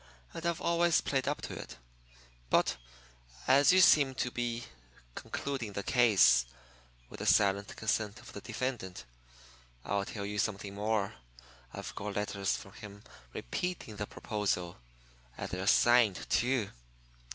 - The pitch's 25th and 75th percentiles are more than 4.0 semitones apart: Yes, average, 4.4 semitones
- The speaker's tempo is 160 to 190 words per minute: No, average, 140 wpm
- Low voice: Yes, low, 105 Hz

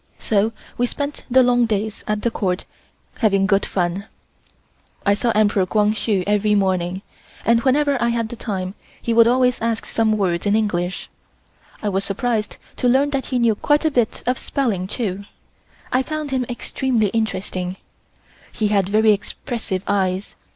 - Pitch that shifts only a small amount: No, average, 3.6 semitones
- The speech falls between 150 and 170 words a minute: Yes, average, 165 wpm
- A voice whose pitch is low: No, high, 215 Hz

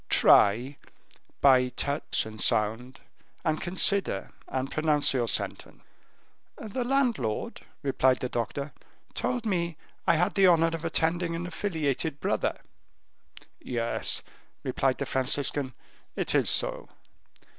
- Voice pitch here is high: No, medium, 145 Hz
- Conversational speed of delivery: No, slow, 115 wpm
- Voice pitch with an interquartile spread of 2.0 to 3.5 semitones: No, average, 5.1 semitones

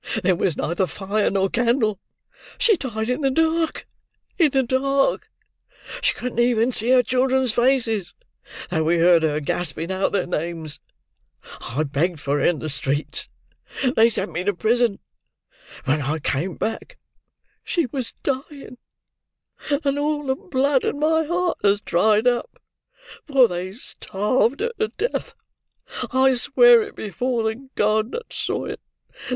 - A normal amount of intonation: No, wide, 6.9 semitones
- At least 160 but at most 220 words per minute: No, average, 150 wpm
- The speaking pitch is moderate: No, high, 235 Hz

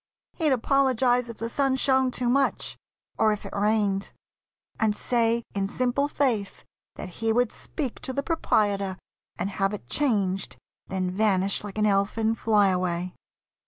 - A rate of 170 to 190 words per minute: No, average, 155 wpm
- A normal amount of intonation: Yes, average, 4.3 semitones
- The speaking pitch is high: Yes, high, 220 Hz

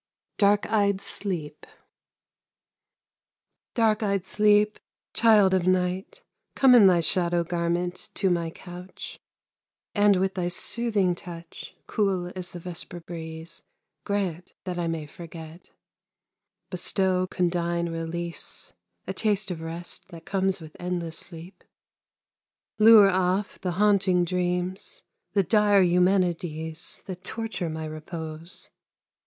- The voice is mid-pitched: Yes, medium, 180 Hz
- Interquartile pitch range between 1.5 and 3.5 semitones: Yes, narrow, 2.6 semitones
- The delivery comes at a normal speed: No, slow, 115 wpm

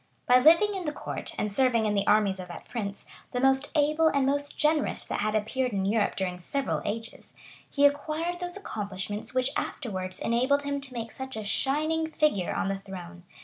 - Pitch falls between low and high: No, very high, 250 Hz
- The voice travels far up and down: Yes, wide, 6.0 semitones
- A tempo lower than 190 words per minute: No, average, 195 wpm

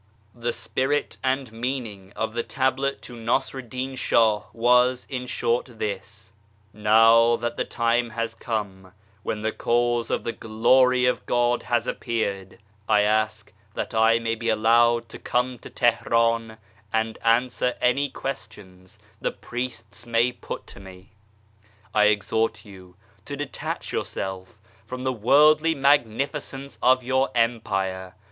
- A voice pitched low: Yes, low, 115 Hz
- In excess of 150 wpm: No, average, 145 wpm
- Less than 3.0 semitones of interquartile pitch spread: Yes, narrow, 2.6 semitones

